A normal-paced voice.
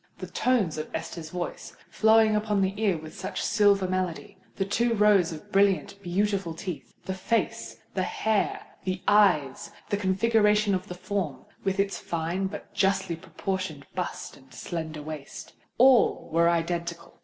No: slow, 130 wpm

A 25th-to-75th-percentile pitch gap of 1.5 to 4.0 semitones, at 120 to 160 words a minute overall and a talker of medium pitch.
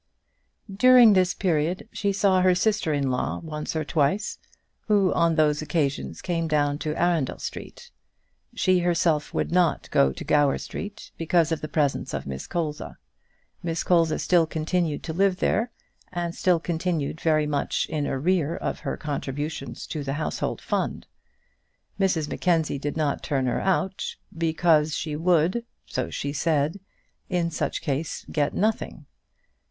Yes: average, 3.3 semitones; average, 150 wpm; medium, 160 Hz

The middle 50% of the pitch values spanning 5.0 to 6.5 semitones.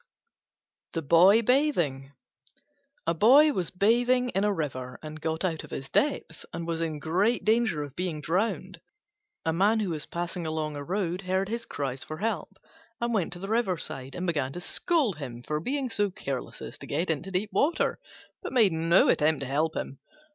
Yes: wide, 5.5 semitones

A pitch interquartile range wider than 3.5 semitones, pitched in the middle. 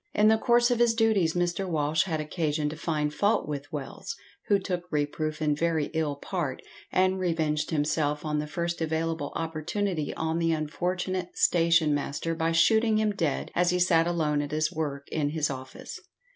No: average, 3.1 semitones; medium, 160 Hz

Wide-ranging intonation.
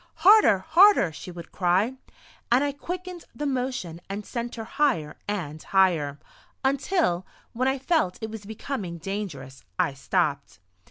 Yes: wide, 8.2 semitones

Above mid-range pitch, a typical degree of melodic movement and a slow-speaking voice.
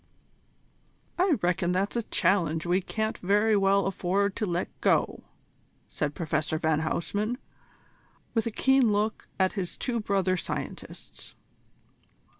Yes: high, 195 Hz; average, 3.5 semitones; slow, 125 wpm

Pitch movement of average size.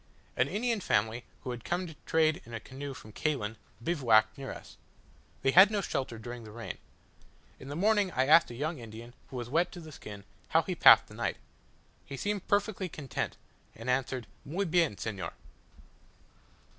No: wide, 6.9 semitones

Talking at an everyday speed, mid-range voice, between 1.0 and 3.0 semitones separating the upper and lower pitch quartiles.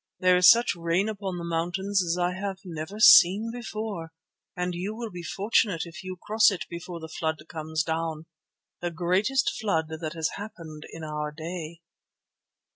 No: average, 170 wpm; medium, 175 Hz; average, 3.6 semitones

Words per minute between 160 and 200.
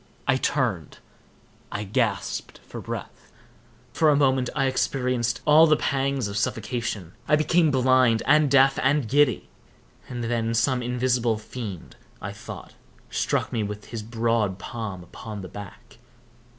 No: slow, 135 wpm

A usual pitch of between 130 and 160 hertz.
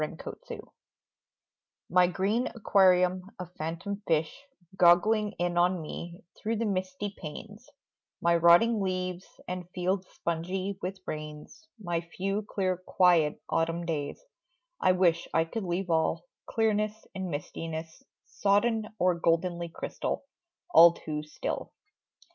No: medium, 180 Hz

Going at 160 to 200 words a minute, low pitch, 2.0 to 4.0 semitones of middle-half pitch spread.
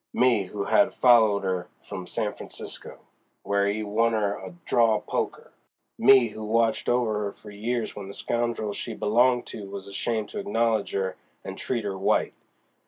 Yes: average, 170 wpm; low, 110 Hz; average, 2.7 semitones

